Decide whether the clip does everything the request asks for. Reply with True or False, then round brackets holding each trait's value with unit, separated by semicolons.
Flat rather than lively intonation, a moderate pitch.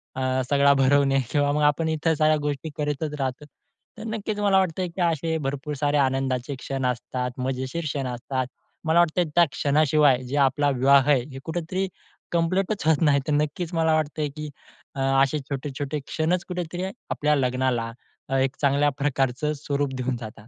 False (3.2 semitones; 145 Hz)